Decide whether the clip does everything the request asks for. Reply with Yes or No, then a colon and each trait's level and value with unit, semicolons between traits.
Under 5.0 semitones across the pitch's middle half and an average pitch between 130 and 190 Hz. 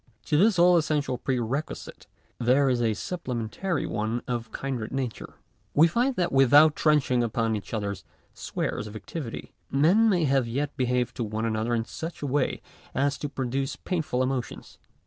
Yes: average, 4.6 semitones; low, 135 Hz